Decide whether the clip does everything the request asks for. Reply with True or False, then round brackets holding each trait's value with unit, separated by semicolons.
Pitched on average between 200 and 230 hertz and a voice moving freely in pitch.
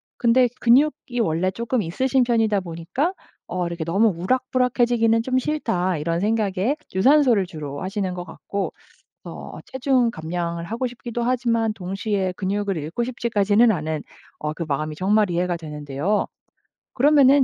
True (205 Hz; 5.8 semitones)